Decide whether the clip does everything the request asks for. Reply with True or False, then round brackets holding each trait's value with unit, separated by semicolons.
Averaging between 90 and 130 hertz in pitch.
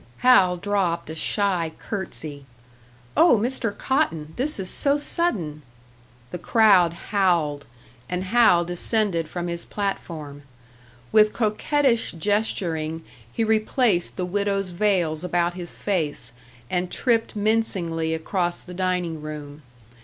False (180 Hz)